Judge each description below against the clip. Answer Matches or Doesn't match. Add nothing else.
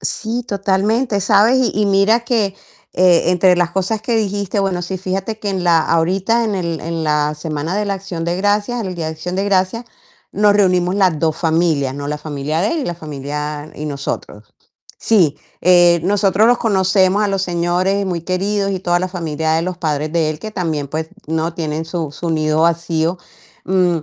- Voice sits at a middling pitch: Matches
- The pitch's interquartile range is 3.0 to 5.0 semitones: Matches